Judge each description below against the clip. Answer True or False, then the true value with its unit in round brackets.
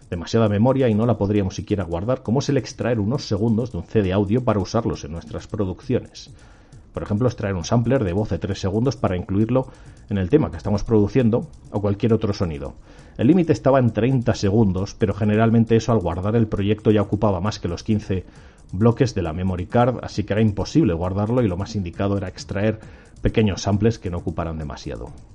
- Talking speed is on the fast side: True (205 wpm)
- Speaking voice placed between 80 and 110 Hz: True (105 Hz)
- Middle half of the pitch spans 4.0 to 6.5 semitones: False (3.2 semitones)